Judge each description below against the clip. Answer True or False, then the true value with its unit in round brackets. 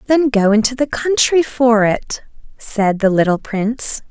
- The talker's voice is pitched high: True (235 Hz)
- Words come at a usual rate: True (160 wpm)